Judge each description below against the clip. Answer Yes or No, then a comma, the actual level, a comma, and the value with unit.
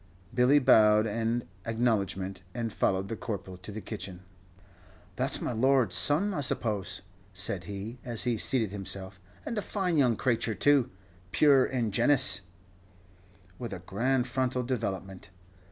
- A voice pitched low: Yes, low, 115 Hz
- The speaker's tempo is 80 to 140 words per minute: Yes, slow, 135 wpm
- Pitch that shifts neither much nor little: Yes, average, 4.6 semitones